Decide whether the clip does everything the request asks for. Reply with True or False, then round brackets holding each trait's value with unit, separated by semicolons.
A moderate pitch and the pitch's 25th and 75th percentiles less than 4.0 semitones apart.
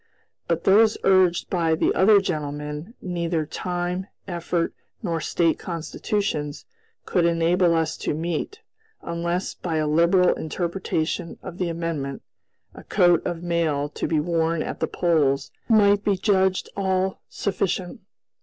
True (170 Hz; 2.5 semitones)